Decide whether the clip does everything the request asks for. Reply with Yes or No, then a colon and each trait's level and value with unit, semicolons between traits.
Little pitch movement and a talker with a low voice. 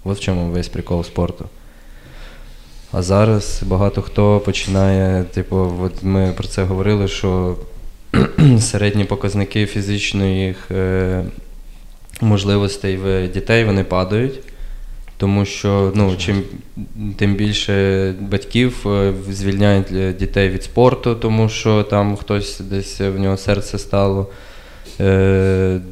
Yes: narrow, 1.4 semitones; low, 100 Hz